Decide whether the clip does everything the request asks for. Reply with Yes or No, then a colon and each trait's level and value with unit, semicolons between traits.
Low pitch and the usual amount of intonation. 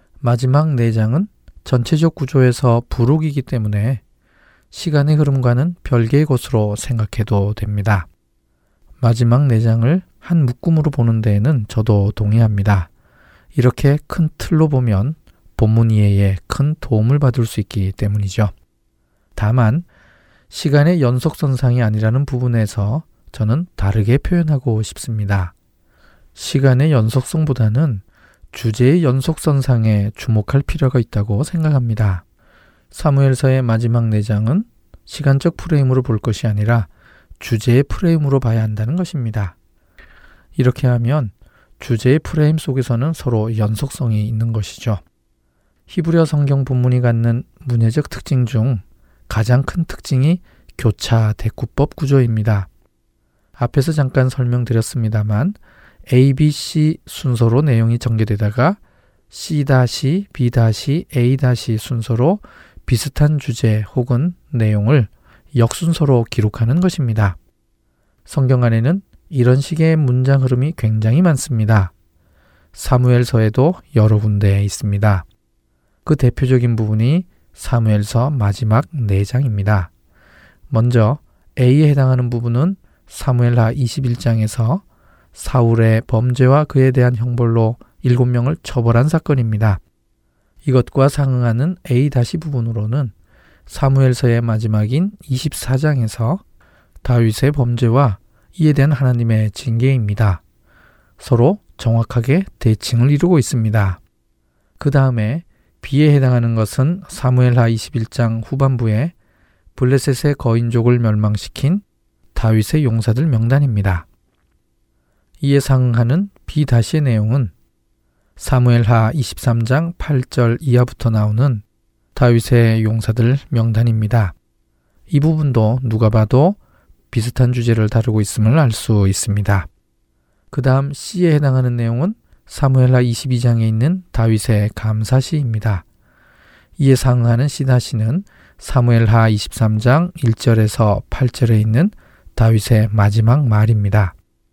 Yes: low, 120 Hz; average, 3.8 semitones